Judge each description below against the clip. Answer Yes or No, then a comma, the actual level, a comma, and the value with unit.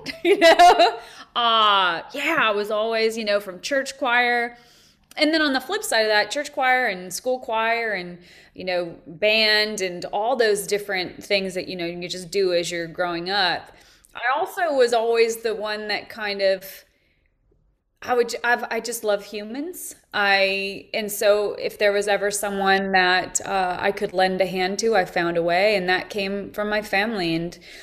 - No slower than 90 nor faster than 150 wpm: No, average, 190 wpm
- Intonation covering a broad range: No, average, 3.7 semitones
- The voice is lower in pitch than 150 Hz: No, high, 205 Hz